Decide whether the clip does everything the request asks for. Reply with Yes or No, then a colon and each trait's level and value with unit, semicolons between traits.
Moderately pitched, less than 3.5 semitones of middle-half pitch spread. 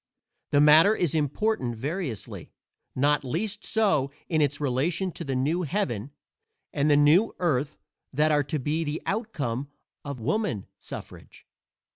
No: medium, 150 Hz; average, 4.4 semitones